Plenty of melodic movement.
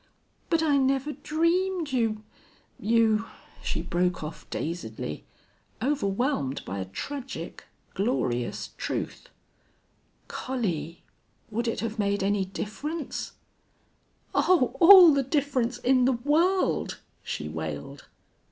Yes: wide, 7.1 semitones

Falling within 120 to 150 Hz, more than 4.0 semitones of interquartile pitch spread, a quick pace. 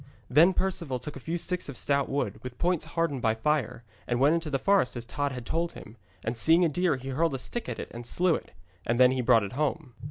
Yes: medium, 140 Hz; average, 5.0 semitones; fast, 255 wpm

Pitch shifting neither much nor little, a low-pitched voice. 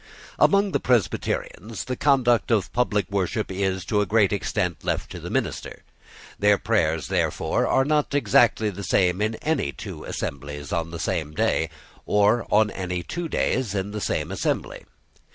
Yes: average, 4.8 semitones; low, 105 Hz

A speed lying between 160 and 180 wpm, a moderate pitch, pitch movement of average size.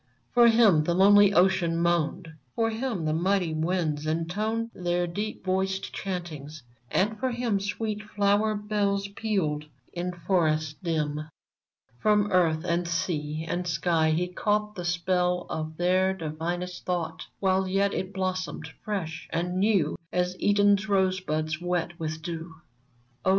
No: average, 140 wpm; medium, 180 Hz; average, 3.5 semitones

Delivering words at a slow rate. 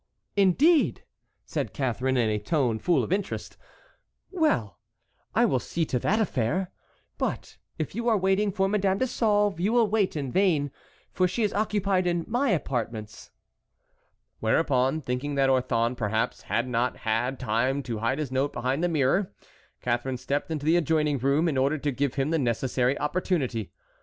No: average, 165 wpm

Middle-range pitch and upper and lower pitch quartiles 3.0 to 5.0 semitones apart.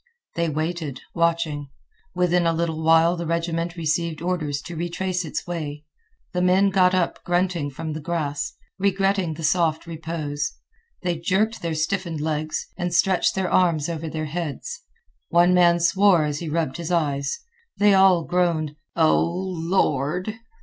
No: medium, 170 Hz; narrow, 2.4 semitones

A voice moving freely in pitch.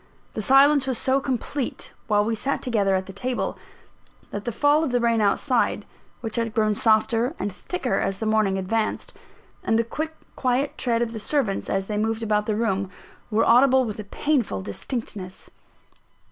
No: average, 3.5 semitones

